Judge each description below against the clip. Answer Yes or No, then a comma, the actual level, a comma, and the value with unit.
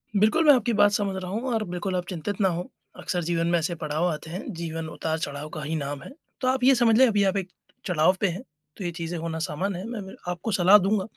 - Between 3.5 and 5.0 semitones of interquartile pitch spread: Yes, average, 3.9 semitones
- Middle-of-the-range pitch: Yes, medium, 180 Hz